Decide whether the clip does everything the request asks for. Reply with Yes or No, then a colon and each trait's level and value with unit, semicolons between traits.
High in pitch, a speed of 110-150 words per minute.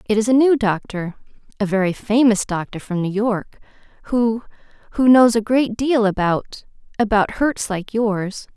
Yes: high, 220 Hz; average, 140 wpm